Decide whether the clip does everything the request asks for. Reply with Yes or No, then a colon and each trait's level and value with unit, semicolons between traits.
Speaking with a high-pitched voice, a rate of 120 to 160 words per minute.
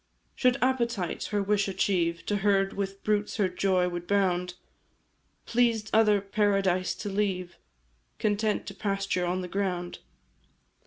Yes: high, 195 Hz; slow, 135 wpm